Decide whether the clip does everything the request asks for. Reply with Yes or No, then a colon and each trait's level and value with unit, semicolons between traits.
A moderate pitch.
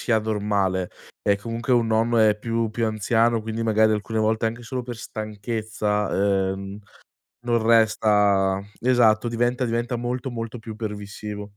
No: low, 110 Hz